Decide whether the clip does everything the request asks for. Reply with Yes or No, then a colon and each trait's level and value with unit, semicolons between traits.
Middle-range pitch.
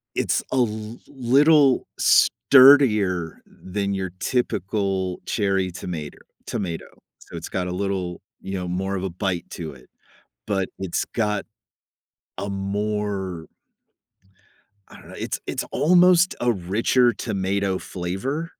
No: low, 100 Hz